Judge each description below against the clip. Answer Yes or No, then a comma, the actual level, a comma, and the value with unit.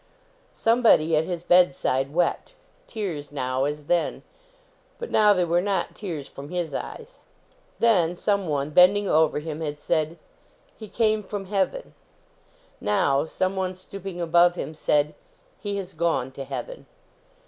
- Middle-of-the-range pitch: Yes, medium, 175 Hz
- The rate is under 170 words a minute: Yes, average, 140 wpm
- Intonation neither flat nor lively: Yes, average, 4.8 semitones